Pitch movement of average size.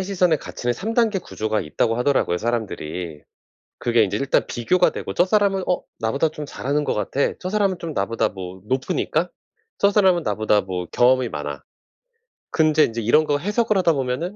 No: wide, 8.7 semitones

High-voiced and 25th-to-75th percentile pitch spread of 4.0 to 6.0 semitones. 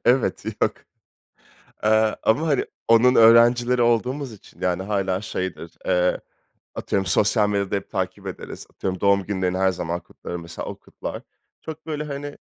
No: low, 105 Hz; average, 4.6 semitones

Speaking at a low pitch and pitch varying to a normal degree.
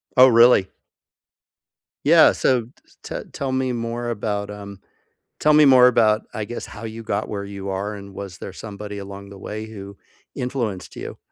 Yes: low, 105 Hz; average, 3.1 semitones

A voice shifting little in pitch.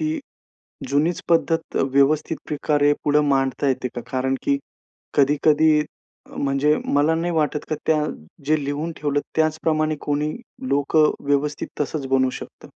Yes: narrow, 1.8 semitones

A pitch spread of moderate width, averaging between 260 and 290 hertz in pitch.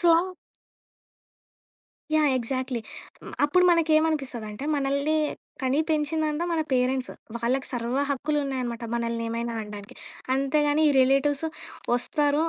Yes: average, 3.7 semitones; very high, 275 Hz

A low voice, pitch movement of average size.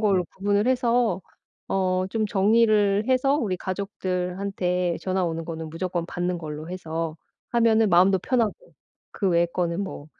No: medium, 185 Hz; average, 3.3 semitones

